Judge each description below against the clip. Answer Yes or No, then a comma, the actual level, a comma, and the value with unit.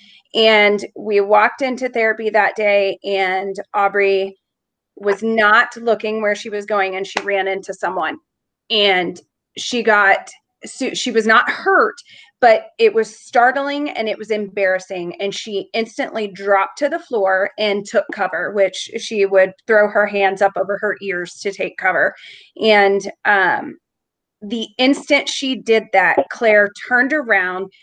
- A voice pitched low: No, high, 210 Hz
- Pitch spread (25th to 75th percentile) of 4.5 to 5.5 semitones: No, average, 3.1 semitones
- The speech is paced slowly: No, average, 150 wpm